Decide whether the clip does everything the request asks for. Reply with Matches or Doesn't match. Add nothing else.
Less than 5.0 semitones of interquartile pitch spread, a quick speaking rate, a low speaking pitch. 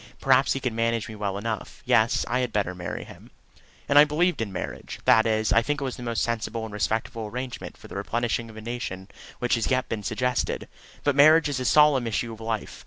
Matches